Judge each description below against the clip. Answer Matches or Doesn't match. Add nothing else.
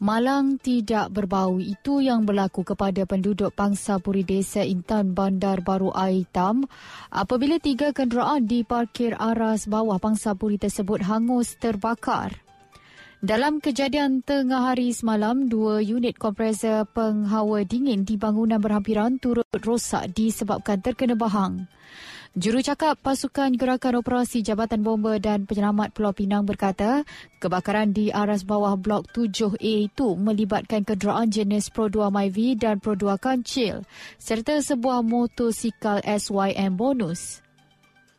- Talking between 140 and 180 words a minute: Doesn't match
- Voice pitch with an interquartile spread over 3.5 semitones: Doesn't match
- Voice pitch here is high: Matches